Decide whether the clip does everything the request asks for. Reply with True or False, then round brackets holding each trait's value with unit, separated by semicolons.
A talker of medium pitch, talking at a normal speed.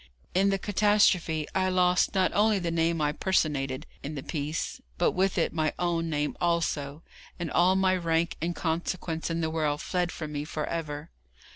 True (165 Hz; 180 wpm)